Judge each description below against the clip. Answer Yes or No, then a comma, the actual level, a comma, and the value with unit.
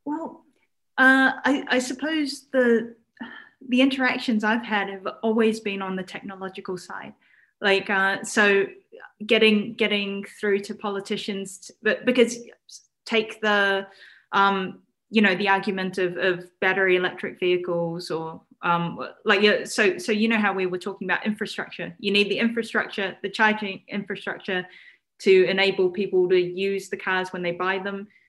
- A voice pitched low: No, high, 200 Hz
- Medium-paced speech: Yes, average, 150 wpm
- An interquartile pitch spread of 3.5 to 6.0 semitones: No, average, 2.9 semitones